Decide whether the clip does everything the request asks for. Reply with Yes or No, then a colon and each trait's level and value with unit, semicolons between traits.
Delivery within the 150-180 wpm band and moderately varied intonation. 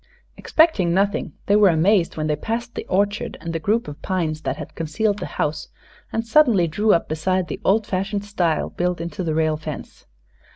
No: average, 195 wpm; average, 4.5 semitones